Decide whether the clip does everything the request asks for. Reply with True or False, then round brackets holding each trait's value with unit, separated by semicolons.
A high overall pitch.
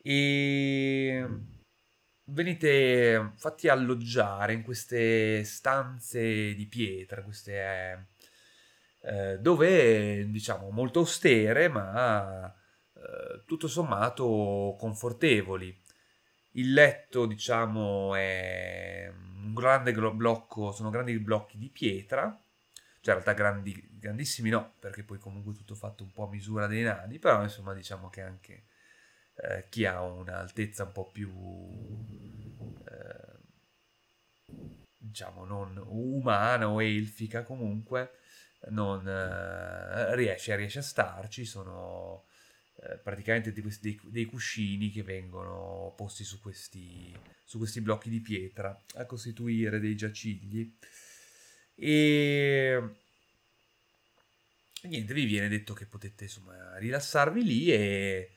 False (110 Hz)